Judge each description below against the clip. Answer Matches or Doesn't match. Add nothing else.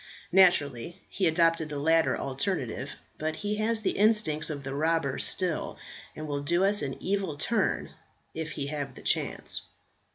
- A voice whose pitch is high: Doesn't match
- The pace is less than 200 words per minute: Matches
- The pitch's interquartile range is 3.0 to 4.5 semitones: Doesn't match